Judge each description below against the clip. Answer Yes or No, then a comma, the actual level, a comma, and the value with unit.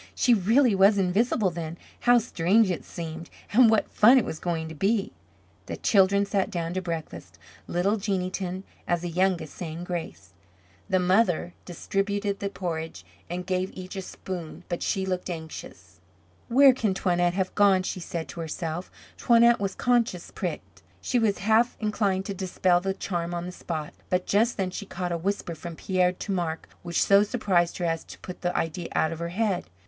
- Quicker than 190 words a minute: No, average, 185 wpm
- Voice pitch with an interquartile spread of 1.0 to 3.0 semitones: Yes, average, 2.7 semitones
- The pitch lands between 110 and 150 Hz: No, medium, 185 Hz